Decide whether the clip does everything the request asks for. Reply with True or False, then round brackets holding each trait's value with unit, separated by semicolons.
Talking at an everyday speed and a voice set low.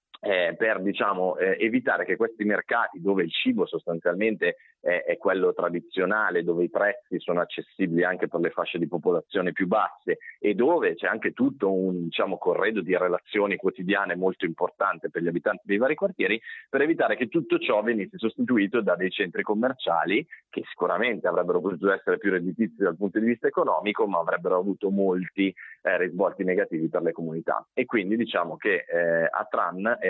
False (175 wpm; 110 Hz)